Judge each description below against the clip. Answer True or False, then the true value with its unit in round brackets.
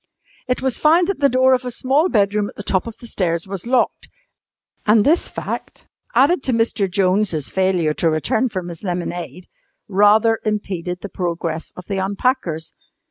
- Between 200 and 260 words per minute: False (175 wpm)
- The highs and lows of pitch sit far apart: True (5.9 semitones)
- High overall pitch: True (205 Hz)